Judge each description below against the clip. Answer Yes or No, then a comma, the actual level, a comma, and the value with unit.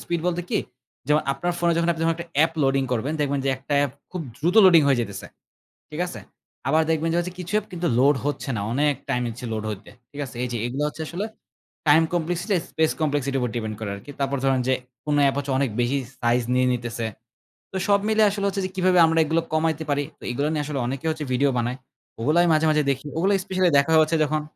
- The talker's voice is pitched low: No, medium, 150 Hz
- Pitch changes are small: No, average, 4.0 semitones